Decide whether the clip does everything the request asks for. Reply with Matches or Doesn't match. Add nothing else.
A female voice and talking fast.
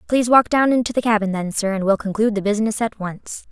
Matches